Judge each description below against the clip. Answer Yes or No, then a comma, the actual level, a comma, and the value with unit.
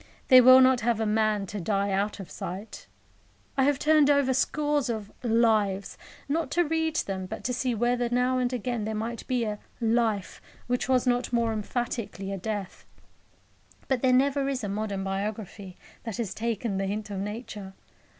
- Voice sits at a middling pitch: No, high, 230 Hz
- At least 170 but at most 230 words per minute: Yes, average, 180 wpm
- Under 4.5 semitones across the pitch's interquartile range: Yes, average, 3.8 semitones